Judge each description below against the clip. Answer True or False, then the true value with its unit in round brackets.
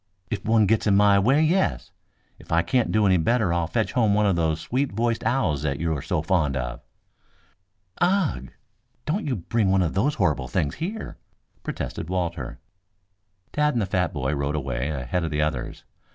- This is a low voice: True (95 Hz)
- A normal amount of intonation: False (7.2 semitones)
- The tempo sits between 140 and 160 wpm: False (190 wpm)